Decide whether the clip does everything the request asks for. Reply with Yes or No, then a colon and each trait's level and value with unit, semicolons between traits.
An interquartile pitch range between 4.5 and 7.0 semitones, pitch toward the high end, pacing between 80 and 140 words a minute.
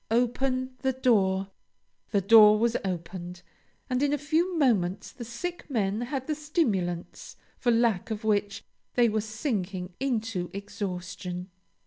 Yes: average, 5.1 semitones; high, 220 Hz; slow, 135 wpm